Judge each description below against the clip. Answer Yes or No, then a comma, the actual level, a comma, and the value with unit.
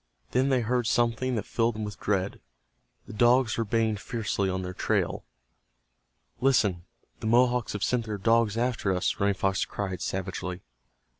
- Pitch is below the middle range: Yes, low, 110 Hz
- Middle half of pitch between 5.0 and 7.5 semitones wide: No, average, 3.6 semitones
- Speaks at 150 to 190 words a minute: Yes, average, 160 wpm